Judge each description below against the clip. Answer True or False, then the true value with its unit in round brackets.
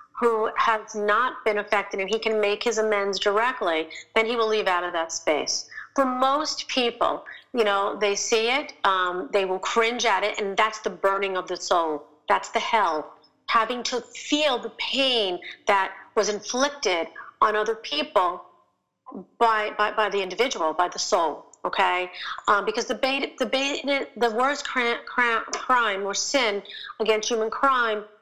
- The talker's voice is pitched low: False (220 Hz)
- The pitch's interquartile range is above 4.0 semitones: False (3.5 semitones)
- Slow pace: False (165 wpm)